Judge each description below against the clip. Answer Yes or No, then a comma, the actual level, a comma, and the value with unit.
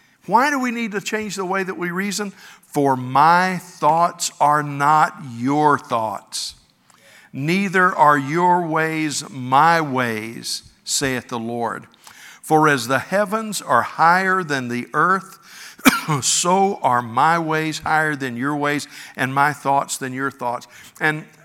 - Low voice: No, medium, 155 Hz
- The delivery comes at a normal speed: Yes, average, 145 wpm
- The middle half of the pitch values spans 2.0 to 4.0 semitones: No, average, 5.2 semitones